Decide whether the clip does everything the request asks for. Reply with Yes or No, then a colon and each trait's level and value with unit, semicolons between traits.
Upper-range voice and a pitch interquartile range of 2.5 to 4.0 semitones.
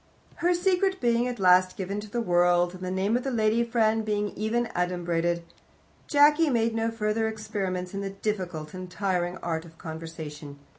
No: high, 200 Hz; average, 4.4 semitones